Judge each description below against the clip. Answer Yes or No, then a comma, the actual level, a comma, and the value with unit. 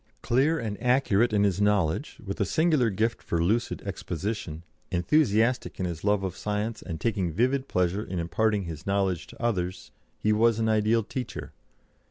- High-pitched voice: No, low, 105 Hz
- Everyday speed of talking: Yes, average, 170 wpm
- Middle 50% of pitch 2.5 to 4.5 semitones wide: Yes, average, 4.1 semitones